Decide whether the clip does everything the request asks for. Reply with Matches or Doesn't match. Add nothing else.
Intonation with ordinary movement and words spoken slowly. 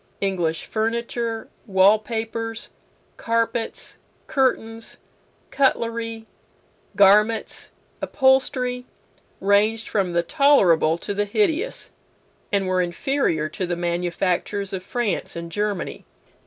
Matches